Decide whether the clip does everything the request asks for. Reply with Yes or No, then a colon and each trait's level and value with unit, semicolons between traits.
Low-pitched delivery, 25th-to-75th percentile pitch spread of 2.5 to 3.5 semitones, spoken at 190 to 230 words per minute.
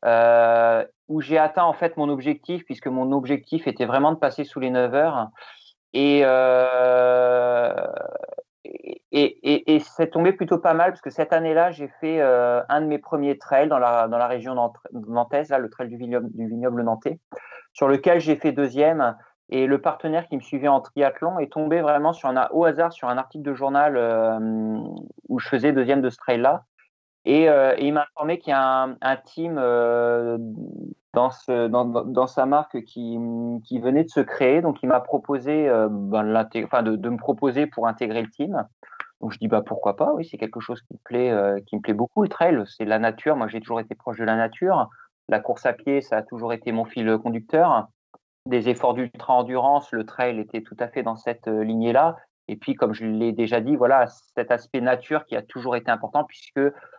No: low, 130 Hz; average, 4.2 semitones; average, 210 wpm